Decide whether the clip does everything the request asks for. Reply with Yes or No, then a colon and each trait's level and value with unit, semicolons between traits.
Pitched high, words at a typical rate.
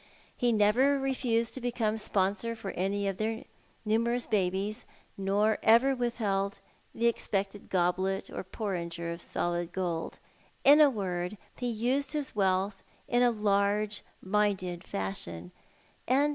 No: high, 210 Hz; slow, 130 wpm